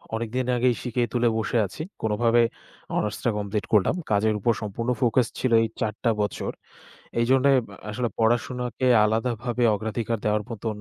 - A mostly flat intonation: Yes, narrow, 2.2 semitones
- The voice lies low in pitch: Yes, low, 115 Hz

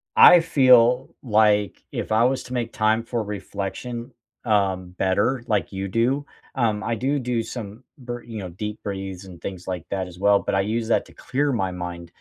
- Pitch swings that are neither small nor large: Yes, average, 3.9 semitones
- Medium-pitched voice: No, low, 110 Hz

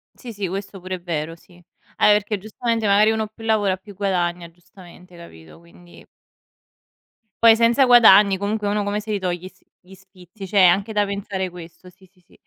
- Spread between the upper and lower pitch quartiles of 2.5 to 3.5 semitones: Yes, average, 2.9 semitones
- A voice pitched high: Yes, high, 195 Hz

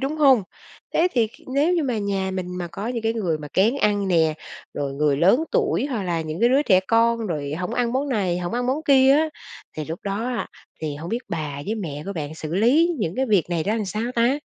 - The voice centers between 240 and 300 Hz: No, high, 205 Hz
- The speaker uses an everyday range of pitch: No, wide, 6.7 semitones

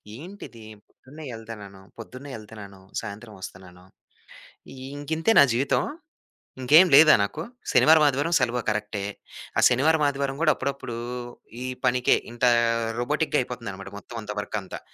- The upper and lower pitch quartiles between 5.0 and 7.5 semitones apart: Yes, wide, 5.4 semitones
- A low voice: Yes, low, 125 Hz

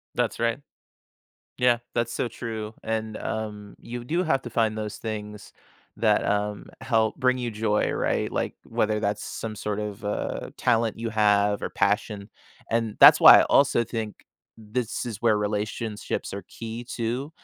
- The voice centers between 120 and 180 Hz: No, low, 110 Hz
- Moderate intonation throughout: No, narrow, 2.0 semitones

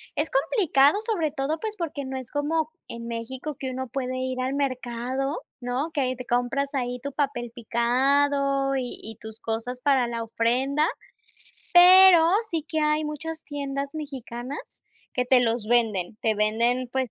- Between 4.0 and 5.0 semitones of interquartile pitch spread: No, average, 3.2 semitones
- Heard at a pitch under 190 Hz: No, very high, 265 Hz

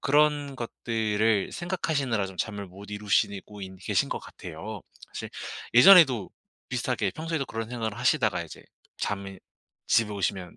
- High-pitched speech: No, low, 110 Hz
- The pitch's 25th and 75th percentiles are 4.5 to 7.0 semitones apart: Yes, average, 5.2 semitones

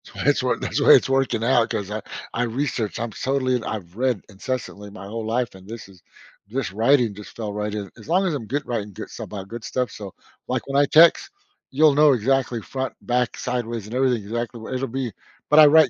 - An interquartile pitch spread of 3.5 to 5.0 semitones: Yes, average, 3.9 semitones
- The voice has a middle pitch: No, low, 120 Hz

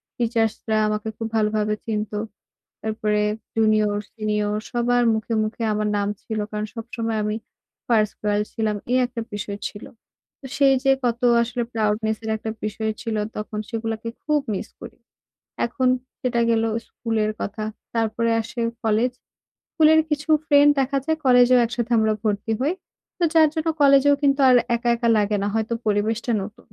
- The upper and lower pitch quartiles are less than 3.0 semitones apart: Yes, narrow, 2.4 semitones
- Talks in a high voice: Yes, high, 225 Hz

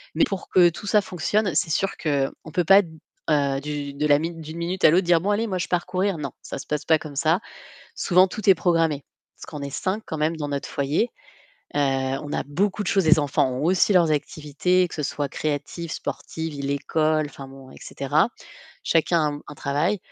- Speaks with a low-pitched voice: No, medium, 160 Hz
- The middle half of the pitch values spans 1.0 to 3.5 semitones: No, average, 3.9 semitones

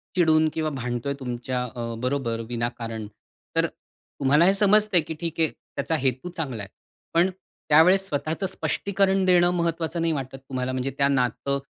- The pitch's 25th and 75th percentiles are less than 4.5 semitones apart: No, average, 5.1 semitones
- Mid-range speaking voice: Yes, medium, 145 Hz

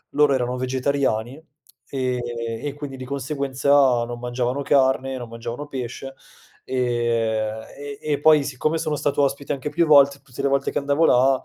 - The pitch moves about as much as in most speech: No, narrow, 2.3 semitones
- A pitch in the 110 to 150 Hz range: Yes, low, 135 Hz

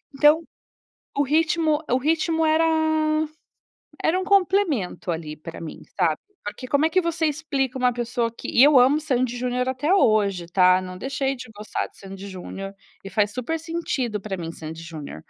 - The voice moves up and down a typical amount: No, wide, 8.0 semitones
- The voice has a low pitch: No, very high, 250 Hz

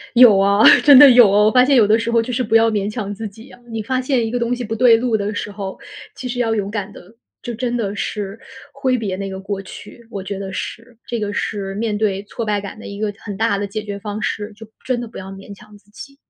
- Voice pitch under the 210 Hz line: No, high, 215 Hz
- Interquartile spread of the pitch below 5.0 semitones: Yes, average, 2.7 semitones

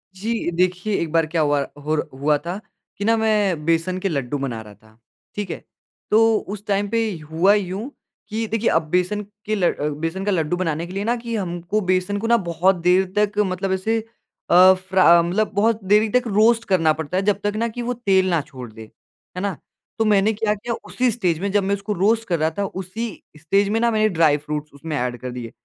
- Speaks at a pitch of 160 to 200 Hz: Yes, high, 190 Hz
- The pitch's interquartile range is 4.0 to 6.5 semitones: Yes, average, 4.3 semitones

